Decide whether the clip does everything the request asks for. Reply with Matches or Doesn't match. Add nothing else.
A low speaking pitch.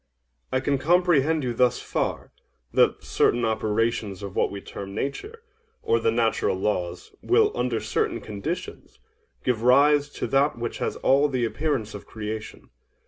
Matches